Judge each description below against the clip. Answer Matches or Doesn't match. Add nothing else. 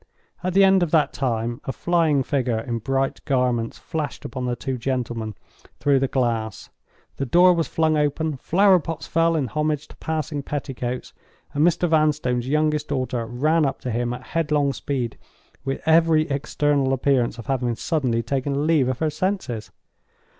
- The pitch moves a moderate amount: Matches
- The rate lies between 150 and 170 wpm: Matches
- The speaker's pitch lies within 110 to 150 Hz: Matches